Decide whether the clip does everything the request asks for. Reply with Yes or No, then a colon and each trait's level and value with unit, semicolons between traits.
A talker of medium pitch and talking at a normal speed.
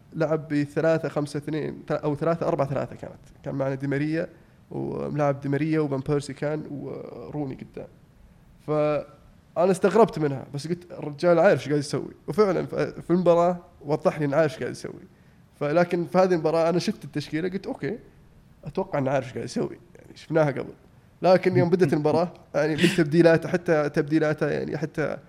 No: medium, 155 Hz; fast, 155 wpm